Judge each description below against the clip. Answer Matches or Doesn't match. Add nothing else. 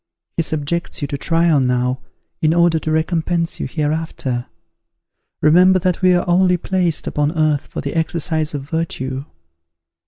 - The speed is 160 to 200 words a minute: Doesn't match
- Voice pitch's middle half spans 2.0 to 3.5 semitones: Matches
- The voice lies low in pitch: Doesn't match